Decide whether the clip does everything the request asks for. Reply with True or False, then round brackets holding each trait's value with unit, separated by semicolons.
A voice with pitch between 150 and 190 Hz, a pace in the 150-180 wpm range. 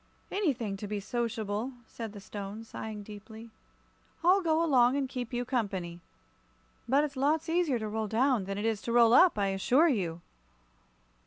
False (230 Hz; 170 wpm)